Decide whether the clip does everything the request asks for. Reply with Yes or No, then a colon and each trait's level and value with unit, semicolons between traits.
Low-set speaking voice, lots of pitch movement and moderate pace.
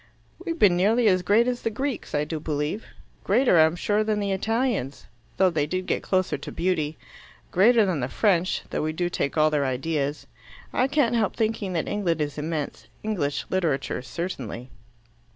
No: medium, 180 Hz; wide, 6.0 semitones; average, 180 wpm